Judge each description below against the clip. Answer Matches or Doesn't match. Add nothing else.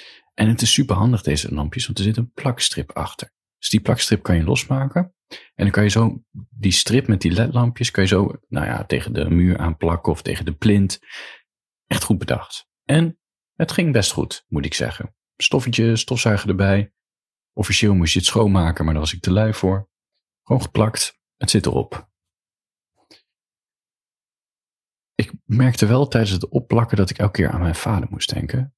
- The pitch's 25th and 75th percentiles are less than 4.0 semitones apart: Doesn't match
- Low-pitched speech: Matches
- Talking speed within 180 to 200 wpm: Matches